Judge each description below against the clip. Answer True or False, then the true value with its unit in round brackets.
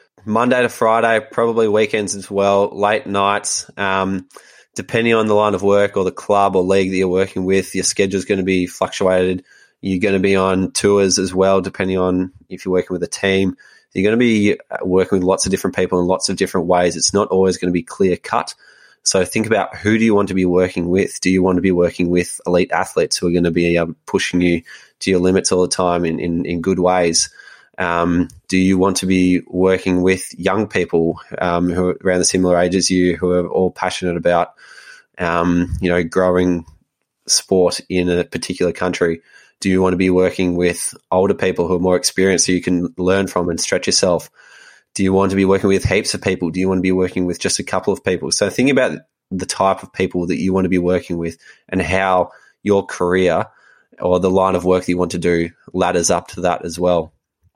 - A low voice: True (95 Hz)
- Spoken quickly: True (230 wpm)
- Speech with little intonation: True (1.3 semitones)